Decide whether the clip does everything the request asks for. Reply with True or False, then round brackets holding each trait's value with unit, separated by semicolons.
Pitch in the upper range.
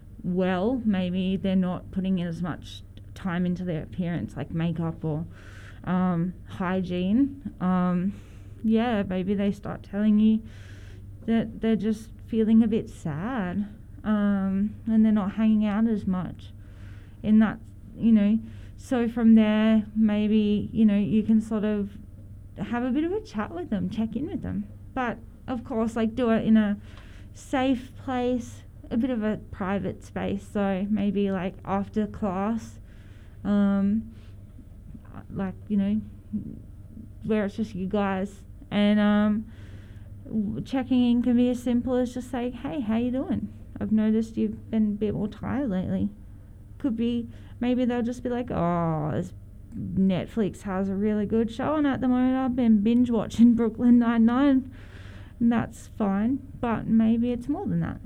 True (205 Hz)